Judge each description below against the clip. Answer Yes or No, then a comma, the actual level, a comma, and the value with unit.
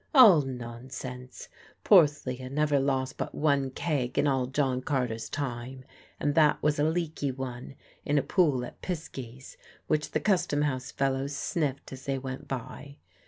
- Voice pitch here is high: No, low, 135 Hz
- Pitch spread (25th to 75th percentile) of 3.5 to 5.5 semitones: No, narrow, 2.5 semitones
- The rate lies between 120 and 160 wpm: Yes, average, 155 wpm